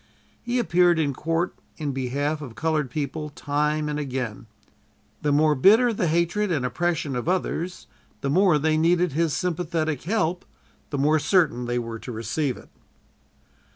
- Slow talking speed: No, average, 155 wpm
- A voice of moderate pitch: Yes, medium, 155 Hz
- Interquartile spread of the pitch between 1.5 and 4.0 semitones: Yes, average, 3.6 semitones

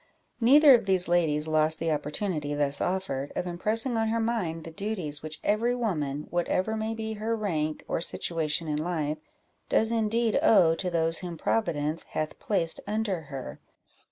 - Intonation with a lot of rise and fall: Yes, wide, 6.0 semitones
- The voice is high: No, medium, 175 Hz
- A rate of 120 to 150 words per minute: No, average, 165 wpm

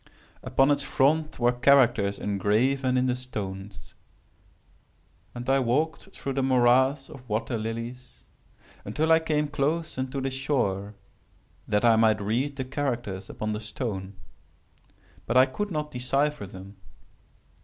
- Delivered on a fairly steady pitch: No, average, 4.2 semitones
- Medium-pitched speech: No, low, 125 Hz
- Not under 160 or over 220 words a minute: No, slow, 135 wpm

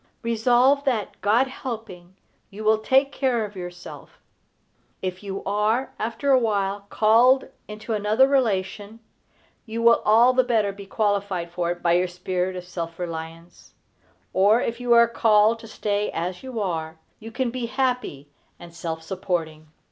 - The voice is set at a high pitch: Yes, high, 210 Hz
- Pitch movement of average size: Yes, average, 4.4 semitones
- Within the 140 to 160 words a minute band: Yes, average, 155 wpm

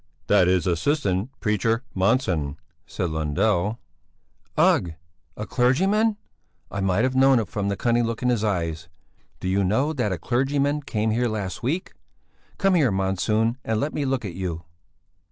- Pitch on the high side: No, low, 110 Hz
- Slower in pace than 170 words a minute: Yes, average, 160 wpm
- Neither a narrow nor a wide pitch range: No, wide, 5.8 semitones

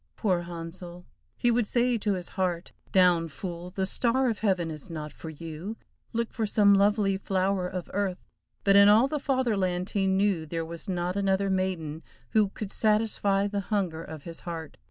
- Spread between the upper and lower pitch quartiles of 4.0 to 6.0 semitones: No, average, 3.1 semitones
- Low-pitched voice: No, high, 190 Hz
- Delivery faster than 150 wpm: Yes, average, 180 wpm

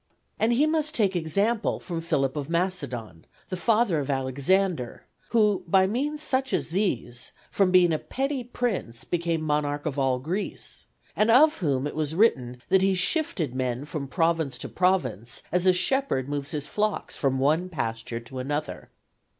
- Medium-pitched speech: Yes, medium, 165 Hz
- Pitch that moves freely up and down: Yes, wide, 6.8 semitones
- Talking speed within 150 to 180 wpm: Yes, average, 165 wpm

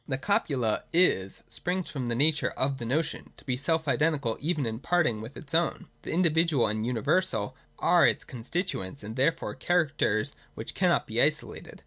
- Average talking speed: Yes, average, 180 wpm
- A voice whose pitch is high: No, medium, 140 Hz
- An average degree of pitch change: No, wide, 6.0 semitones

